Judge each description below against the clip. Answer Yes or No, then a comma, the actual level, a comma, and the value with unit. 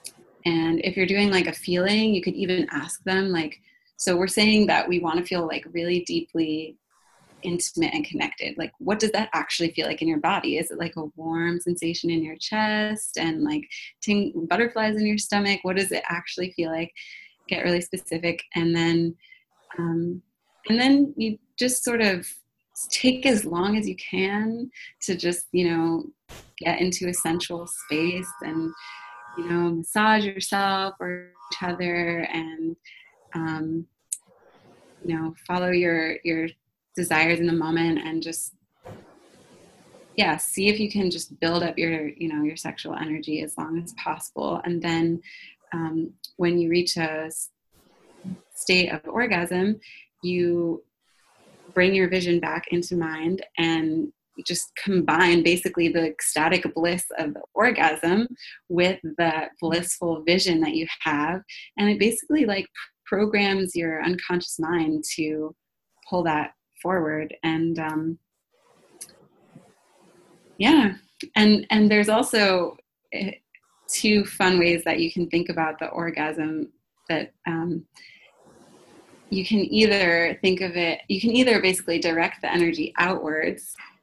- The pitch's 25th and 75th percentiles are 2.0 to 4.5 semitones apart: Yes, average, 3.2 semitones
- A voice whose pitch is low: No, medium, 175 Hz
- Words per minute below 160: Yes, average, 145 wpm